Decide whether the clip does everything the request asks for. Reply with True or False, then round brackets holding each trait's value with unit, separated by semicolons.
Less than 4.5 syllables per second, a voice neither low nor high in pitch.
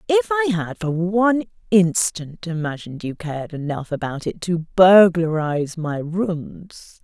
True (4.3 syllables/s; 180 Hz)